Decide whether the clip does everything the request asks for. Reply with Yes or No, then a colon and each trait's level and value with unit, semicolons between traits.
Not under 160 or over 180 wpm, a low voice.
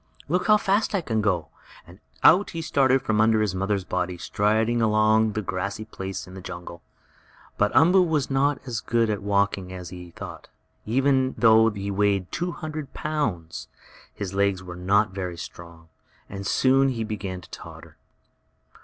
Yes: average, 170 wpm; low, 105 Hz